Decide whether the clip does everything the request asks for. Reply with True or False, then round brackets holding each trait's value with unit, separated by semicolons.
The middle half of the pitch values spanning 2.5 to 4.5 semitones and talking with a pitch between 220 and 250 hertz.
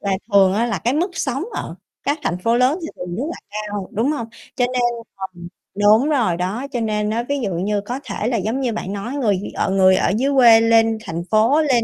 True (4.1 semitones; 225 Hz)